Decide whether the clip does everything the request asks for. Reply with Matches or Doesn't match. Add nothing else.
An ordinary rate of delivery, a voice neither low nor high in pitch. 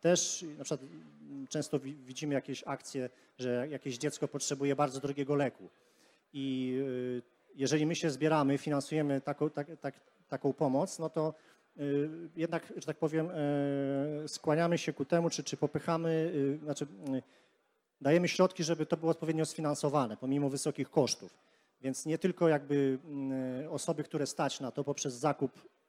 Matches